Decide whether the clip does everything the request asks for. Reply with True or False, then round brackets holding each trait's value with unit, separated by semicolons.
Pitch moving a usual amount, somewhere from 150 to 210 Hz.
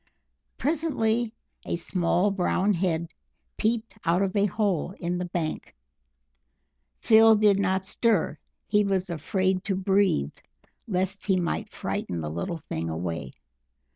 True (3.5 semitones; 190 Hz)